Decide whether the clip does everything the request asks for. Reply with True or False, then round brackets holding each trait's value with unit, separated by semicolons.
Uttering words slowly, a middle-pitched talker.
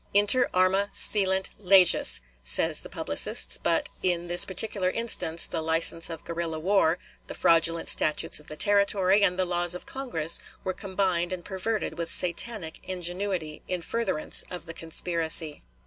False (150 wpm; 180 Hz)